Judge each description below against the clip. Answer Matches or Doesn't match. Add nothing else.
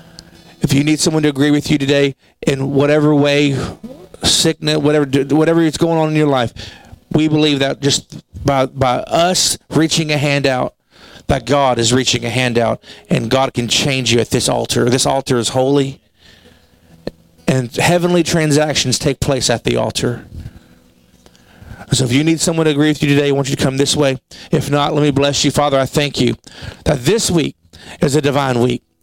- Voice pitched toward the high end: Doesn't match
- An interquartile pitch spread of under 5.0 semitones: Matches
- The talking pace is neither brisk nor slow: Matches